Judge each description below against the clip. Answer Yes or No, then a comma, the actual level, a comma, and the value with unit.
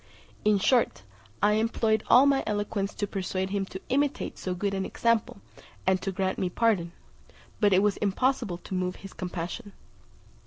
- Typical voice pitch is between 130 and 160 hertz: No, high, 200 Hz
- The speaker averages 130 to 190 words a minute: Yes, average, 165 wpm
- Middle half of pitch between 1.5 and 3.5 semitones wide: Yes, average, 2.9 semitones